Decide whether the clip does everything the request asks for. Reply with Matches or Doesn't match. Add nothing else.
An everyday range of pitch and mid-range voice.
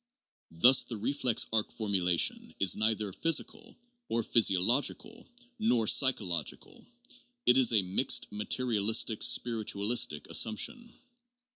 Doesn't match